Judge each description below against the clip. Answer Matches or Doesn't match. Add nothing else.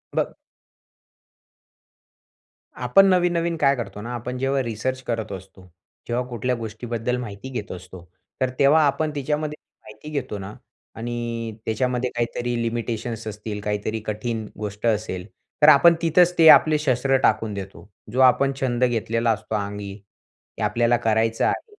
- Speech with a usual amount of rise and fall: Matches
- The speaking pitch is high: Doesn't match